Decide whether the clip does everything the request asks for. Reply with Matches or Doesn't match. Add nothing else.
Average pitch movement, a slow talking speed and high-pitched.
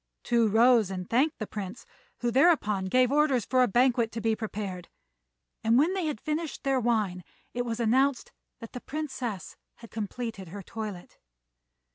Doesn't match